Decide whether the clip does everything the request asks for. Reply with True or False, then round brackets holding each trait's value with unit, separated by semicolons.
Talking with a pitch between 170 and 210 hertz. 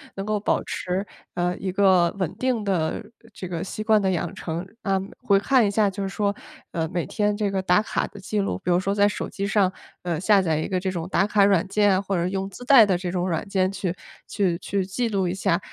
True (195 Hz)